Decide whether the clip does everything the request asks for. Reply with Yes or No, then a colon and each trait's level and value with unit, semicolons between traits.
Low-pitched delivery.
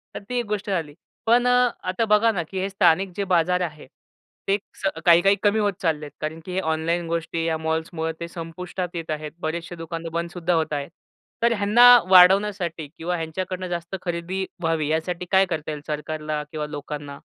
No: medium, 170 Hz